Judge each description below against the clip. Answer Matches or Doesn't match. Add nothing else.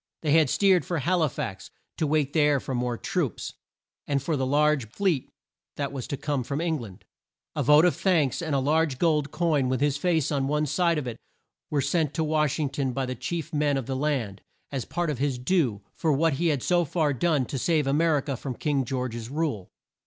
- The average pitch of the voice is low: Doesn't match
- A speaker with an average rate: Doesn't match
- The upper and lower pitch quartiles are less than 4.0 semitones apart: Matches